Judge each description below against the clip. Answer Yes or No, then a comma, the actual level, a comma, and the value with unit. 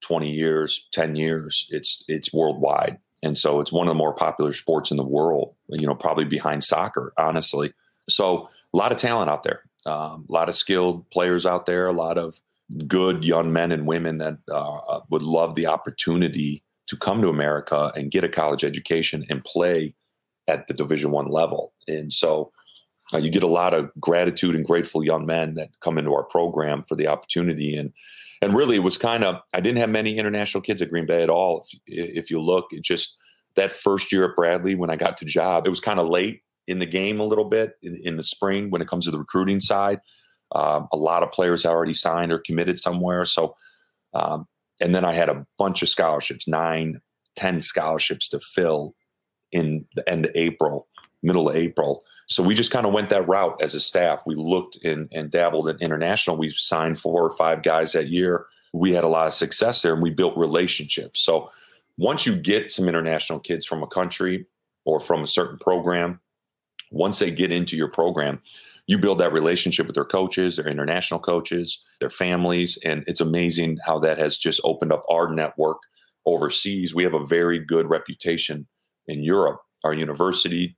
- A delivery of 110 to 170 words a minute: No, average, 200 wpm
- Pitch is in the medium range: No, very low, 85 Hz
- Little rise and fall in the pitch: Yes, narrow, 2.3 semitones